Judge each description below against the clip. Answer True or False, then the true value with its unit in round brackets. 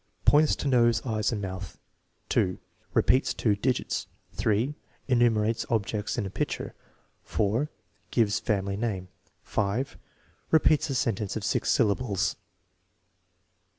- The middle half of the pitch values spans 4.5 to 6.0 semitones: False (3.6 semitones)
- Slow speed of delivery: True (120 wpm)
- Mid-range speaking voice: False (110 Hz)